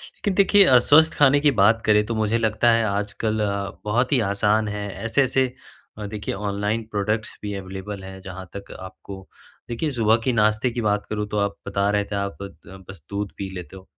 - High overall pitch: No, low, 105 Hz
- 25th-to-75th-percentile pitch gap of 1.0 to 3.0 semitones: Yes, narrow, 2.5 semitones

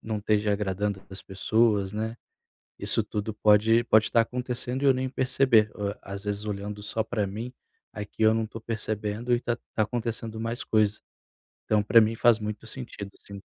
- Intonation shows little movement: Yes, narrow, 2.0 semitones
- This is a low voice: Yes, low, 110 Hz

